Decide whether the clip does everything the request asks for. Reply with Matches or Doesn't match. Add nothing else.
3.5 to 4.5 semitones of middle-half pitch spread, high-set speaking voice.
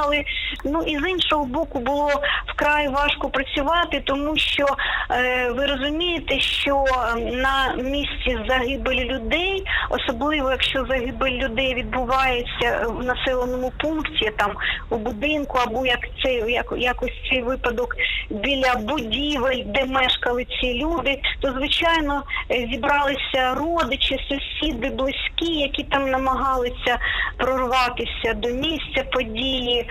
Doesn't match